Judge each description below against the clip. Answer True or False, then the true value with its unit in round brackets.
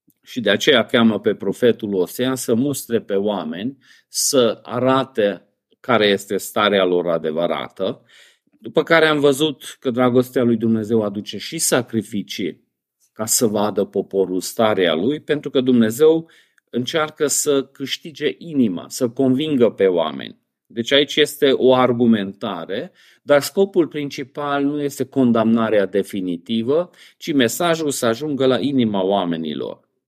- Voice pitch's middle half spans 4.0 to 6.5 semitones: True (5.0 semitones)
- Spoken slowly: False (130 wpm)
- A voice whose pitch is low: True (125 Hz)